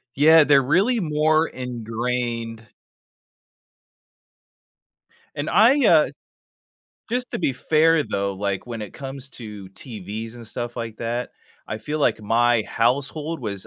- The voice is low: Yes, low, 125 Hz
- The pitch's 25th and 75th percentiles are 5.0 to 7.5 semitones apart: Yes, average, 5.3 semitones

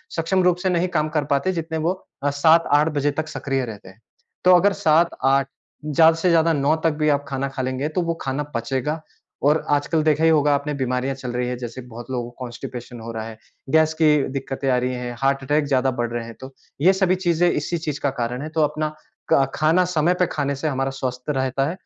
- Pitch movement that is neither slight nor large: Yes, average, 3.7 semitones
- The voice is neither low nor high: Yes, medium, 145 Hz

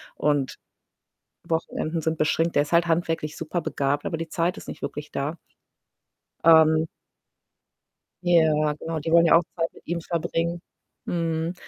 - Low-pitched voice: No, medium, 165 Hz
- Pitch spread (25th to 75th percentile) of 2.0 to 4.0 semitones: No, narrow, 1.6 semitones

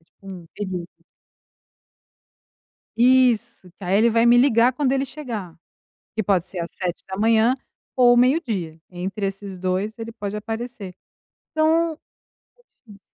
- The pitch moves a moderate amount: Yes, average, 4.4 semitones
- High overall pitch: Yes, high, 220 Hz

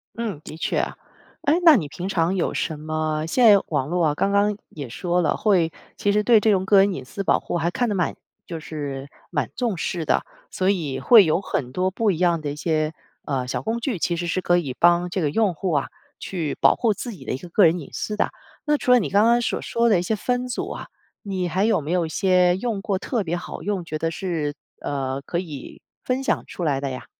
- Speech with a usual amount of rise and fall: Yes, average, 4.8 semitones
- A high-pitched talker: No, medium, 180 Hz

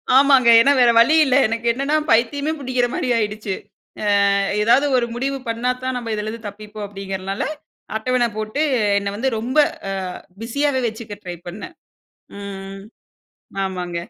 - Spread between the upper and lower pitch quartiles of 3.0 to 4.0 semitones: Yes, average, 3.7 semitones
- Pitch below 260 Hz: Yes, high, 230 Hz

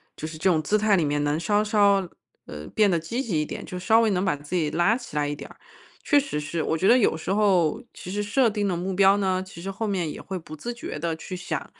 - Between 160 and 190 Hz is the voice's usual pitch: Yes, medium, 185 Hz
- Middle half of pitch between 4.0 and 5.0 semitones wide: Yes, average, 4.5 semitones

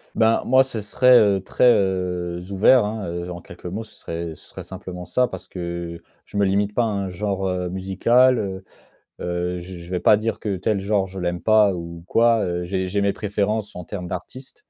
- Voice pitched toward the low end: Yes, very low, 95 Hz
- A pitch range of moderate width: Yes, average, 3.2 semitones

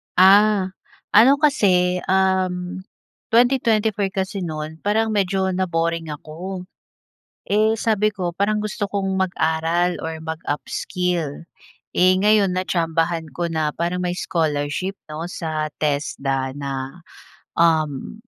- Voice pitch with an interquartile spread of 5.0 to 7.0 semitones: No, average, 3.5 semitones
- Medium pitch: Yes, medium, 180 Hz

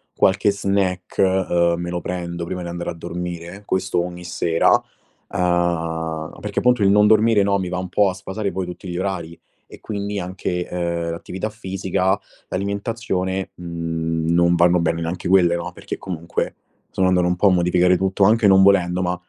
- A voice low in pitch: Yes, very low, 90 Hz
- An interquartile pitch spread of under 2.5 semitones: Yes, narrow, 2.0 semitones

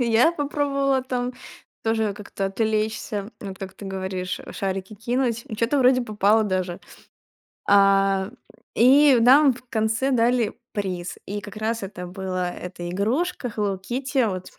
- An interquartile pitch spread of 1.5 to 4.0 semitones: No, average, 4.4 semitones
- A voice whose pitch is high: Yes, high, 215 Hz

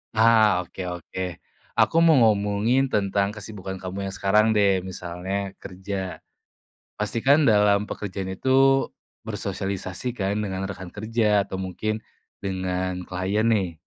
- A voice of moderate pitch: No, low, 100 Hz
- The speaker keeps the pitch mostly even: Yes, narrow, 2.3 semitones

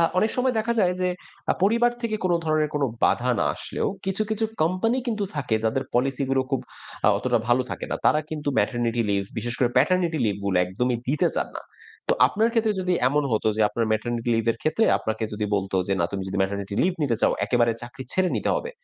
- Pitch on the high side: No, low, 135 Hz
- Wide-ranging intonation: Yes, wide, 8.1 semitones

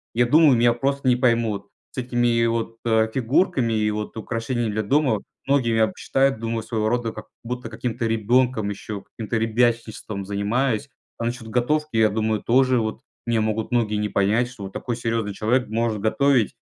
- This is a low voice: Yes, low, 115 Hz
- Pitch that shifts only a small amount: Yes, narrow, 2.1 semitones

